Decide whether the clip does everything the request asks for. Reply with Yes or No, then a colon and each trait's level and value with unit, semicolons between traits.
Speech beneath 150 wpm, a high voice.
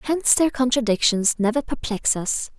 Yes: average, 140 wpm; high, 240 Hz